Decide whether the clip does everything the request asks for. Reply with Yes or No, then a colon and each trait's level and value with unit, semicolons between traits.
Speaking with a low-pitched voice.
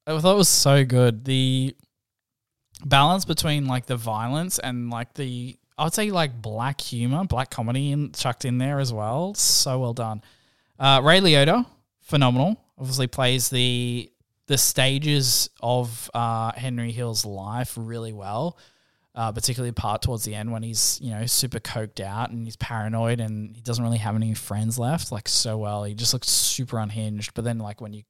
Yes: low, 120 Hz